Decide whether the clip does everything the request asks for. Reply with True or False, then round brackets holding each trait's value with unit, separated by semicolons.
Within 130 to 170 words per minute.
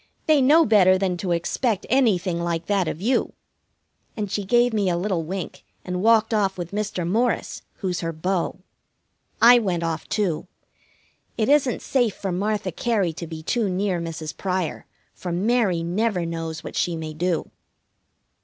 True (165 wpm)